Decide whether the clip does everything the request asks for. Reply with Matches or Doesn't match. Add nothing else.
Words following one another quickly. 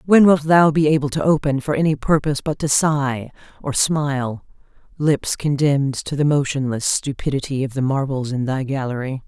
Doesn't match